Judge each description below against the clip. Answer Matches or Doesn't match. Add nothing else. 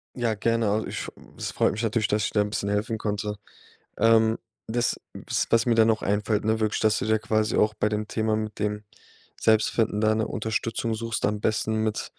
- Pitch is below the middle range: Matches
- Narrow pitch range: Matches